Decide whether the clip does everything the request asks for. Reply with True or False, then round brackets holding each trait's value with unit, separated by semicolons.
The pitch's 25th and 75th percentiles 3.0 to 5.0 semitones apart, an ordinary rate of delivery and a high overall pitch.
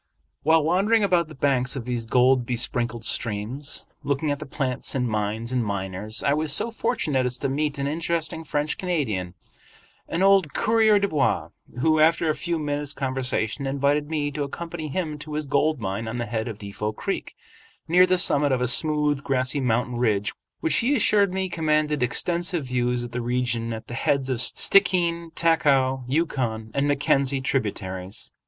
False (4.6 semitones; 175 wpm; 140 Hz)